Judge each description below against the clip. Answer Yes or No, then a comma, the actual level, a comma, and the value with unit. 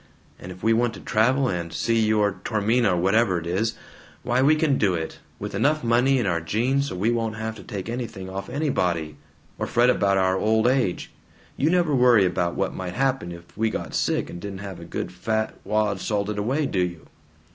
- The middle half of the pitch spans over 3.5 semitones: Yes, average, 4.6 semitones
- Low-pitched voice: Yes, low, 110 Hz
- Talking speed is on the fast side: Yes, fast, 210 wpm